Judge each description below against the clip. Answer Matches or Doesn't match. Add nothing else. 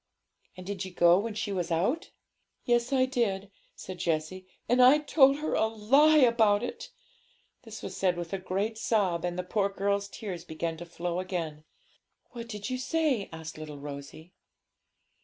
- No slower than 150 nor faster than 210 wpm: Matches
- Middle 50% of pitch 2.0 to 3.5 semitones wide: Doesn't match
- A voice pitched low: Doesn't match